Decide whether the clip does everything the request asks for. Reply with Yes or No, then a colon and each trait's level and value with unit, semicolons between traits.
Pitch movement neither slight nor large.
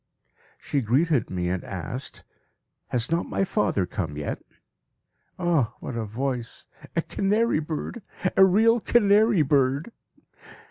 No: wide, 8.9 semitones